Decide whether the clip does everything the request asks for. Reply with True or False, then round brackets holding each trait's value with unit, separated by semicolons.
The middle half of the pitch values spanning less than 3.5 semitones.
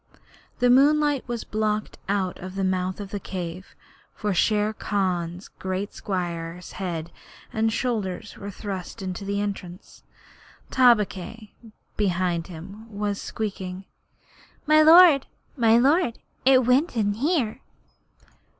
False (4.1 semitones)